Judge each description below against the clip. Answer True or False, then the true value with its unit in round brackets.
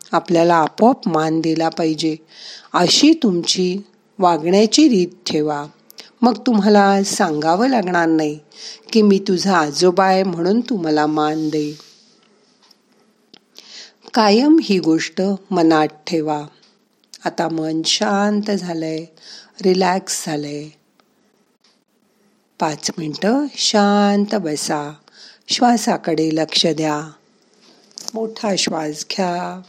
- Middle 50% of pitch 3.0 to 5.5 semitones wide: True (5.1 semitones)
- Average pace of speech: True (90 wpm)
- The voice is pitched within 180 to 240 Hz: True (190 Hz)